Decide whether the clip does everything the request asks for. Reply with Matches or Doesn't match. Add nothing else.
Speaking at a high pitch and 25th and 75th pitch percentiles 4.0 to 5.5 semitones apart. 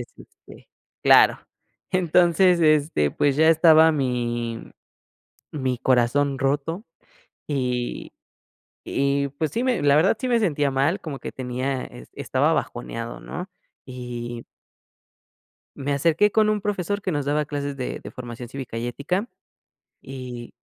Doesn't match